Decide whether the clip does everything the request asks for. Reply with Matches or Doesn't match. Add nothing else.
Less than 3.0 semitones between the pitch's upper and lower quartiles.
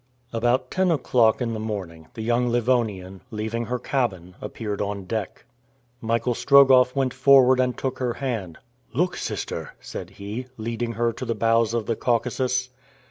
Matches